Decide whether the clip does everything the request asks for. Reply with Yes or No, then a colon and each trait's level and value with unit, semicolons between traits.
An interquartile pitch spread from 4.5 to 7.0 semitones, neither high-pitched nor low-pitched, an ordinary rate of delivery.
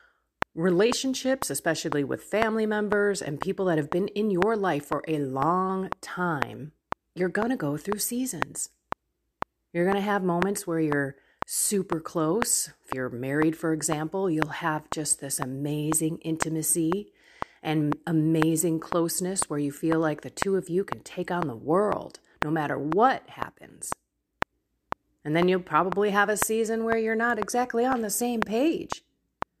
Yes: average, 5.0 semitones; medium, 175 Hz; average, 160 wpm